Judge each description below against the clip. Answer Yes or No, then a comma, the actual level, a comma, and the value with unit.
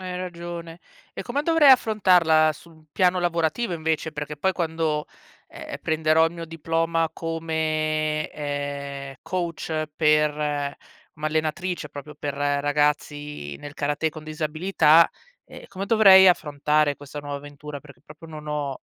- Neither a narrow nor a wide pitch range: No, narrow, 2.2 semitones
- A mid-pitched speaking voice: Yes, medium, 155 Hz